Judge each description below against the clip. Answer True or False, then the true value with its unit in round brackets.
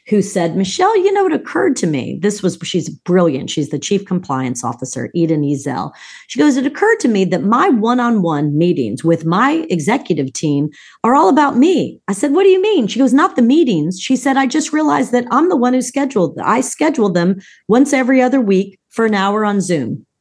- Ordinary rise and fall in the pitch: False (7.9 semitones)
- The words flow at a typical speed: False (215 wpm)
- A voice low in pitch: False (210 Hz)